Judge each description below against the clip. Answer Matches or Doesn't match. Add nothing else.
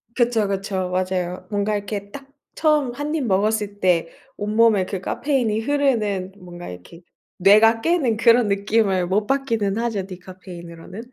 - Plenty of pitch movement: Doesn't match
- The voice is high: Matches